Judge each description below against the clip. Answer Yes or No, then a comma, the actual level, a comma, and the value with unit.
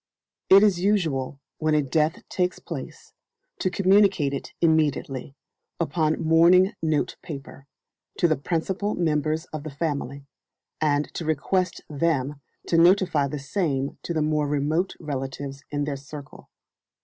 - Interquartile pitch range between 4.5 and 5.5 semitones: No, average, 3.3 semitones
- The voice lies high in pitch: No, medium, 155 Hz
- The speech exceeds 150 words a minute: No, slow, 135 wpm